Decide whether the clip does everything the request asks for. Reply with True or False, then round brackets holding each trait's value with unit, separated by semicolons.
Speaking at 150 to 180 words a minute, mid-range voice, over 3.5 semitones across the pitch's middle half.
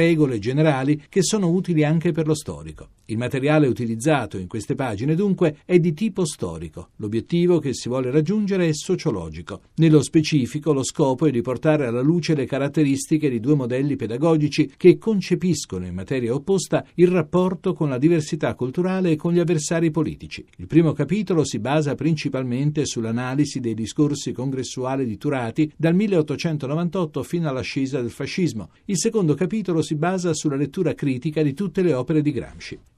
True (165 wpm; 150 Hz; 4.6 semitones)